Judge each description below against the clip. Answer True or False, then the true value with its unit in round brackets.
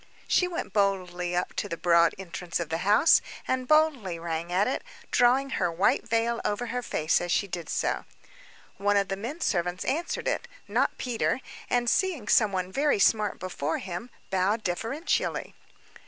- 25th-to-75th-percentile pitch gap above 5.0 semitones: True (5.6 semitones)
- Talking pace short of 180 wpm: True (170 wpm)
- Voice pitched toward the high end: True (200 Hz)